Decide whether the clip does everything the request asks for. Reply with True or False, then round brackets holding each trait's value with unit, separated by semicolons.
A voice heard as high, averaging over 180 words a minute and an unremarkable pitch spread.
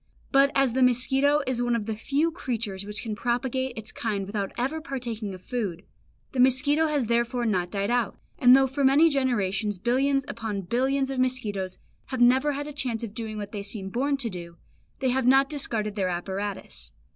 True (240 Hz; 195 wpm; 4.5 semitones)